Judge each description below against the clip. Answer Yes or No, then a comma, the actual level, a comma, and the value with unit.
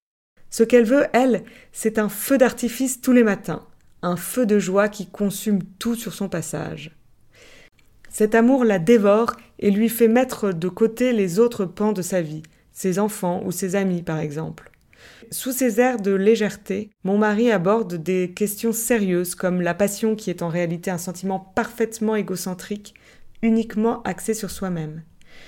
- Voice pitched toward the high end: Yes, high, 205 Hz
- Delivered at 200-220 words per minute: No, average, 165 wpm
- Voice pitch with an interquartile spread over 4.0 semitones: No, average, 3.7 semitones